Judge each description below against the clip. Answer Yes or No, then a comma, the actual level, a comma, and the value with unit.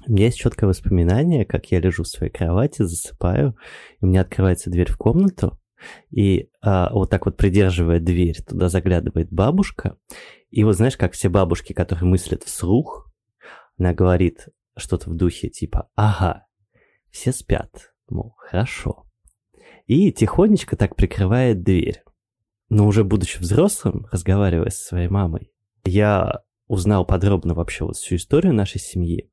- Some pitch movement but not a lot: Yes, average, 3.3 semitones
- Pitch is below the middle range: Yes, very low, 95 Hz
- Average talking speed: Yes, average, 145 wpm